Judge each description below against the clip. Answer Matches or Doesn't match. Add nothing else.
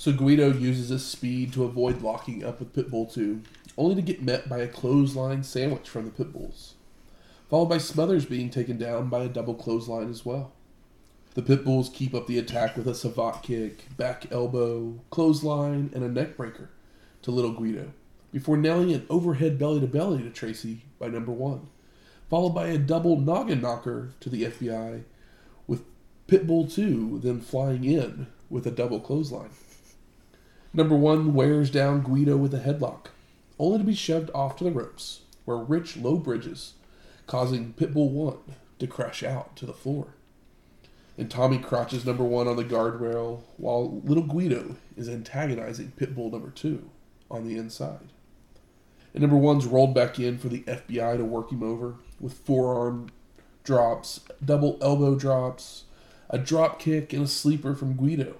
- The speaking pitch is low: Matches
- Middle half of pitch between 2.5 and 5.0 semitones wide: Matches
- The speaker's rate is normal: Matches